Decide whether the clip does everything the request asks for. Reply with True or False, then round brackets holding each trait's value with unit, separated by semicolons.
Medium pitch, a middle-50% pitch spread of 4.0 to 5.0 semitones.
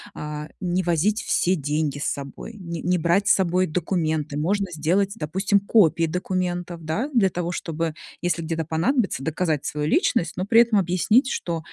False (175 Hz; 3.4 semitones)